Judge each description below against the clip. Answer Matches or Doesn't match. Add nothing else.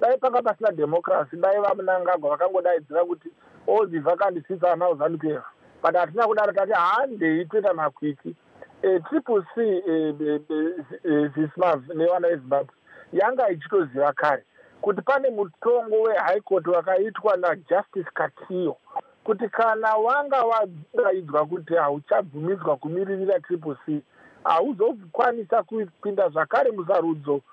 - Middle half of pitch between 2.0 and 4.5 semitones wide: Doesn't match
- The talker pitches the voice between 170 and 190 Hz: Matches